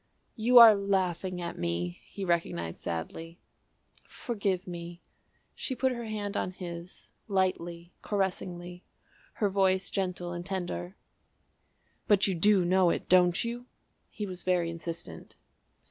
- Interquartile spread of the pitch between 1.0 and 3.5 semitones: Yes, narrow, 2.6 semitones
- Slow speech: Yes, slow, 130 wpm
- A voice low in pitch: No, medium, 185 Hz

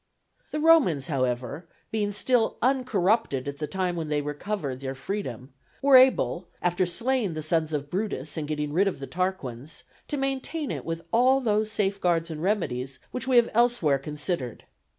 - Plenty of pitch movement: Yes, wide, 7.3 semitones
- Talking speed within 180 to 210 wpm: No, average, 170 wpm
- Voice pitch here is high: No, medium, 175 Hz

